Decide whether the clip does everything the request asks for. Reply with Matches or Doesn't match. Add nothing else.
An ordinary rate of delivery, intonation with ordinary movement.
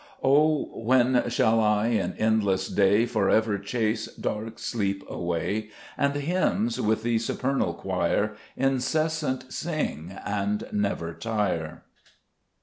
Doesn't match